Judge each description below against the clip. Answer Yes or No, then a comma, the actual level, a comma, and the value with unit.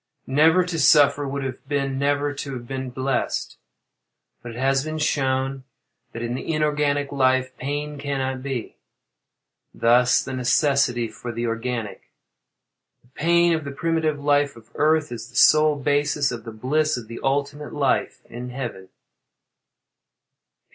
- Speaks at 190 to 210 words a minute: No, average, 150 wpm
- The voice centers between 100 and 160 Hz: Yes, low, 135 Hz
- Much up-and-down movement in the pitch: No, average, 2.8 semitones